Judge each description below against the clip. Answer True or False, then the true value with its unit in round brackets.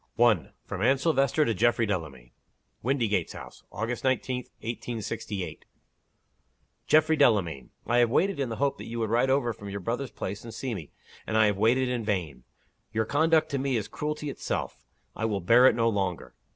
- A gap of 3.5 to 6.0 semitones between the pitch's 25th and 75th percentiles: True (4.4 semitones)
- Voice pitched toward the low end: True (115 Hz)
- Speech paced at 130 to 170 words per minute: False (185 wpm)